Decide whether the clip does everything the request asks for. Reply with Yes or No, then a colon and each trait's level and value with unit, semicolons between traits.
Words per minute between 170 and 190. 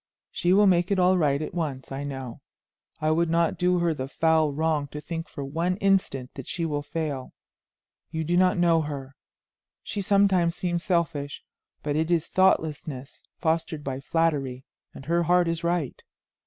Yes: average, 175 wpm